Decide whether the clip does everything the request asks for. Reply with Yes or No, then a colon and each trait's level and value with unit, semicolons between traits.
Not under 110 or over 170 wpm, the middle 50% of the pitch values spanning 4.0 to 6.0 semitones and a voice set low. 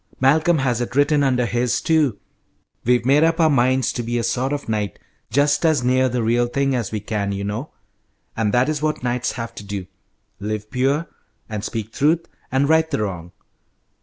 No: average, 195 wpm; average, 4.4 semitones; low, 125 Hz